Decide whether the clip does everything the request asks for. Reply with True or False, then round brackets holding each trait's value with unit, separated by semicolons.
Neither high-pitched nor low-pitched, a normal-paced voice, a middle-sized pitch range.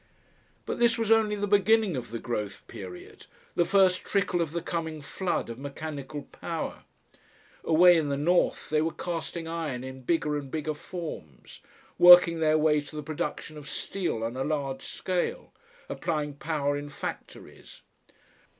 True (155 Hz; 160 wpm; 3.6 semitones)